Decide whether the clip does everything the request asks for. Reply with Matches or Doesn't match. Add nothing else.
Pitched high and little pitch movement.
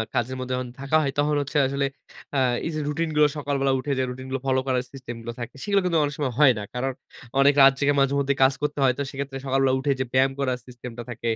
Doesn't match